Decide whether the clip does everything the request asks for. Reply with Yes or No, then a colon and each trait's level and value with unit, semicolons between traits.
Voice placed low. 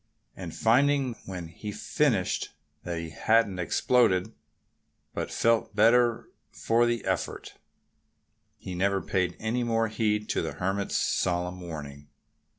Yes: low, 105 Hz